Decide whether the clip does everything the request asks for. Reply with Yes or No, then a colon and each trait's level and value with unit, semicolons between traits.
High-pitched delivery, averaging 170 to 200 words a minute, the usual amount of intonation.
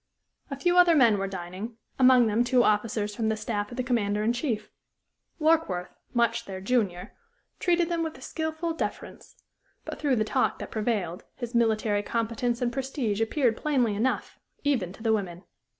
Yes: high, 235 Hz; average, 175 wpm; average, 3.9 semitones